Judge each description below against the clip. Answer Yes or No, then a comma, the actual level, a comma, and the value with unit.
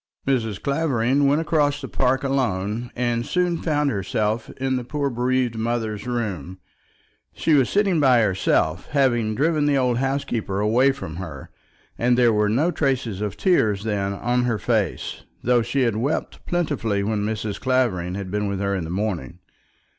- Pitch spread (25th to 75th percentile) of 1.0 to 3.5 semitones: No, average, 4.6 semitones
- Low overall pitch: Yes, low, 120 Hz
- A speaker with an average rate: Yes, average, 170 wpm